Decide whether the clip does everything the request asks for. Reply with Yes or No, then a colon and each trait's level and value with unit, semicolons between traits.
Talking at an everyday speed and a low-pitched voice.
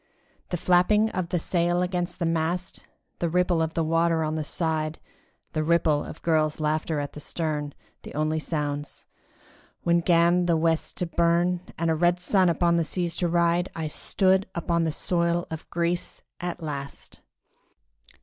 No: average, 165 wpm; medium, 170 Hz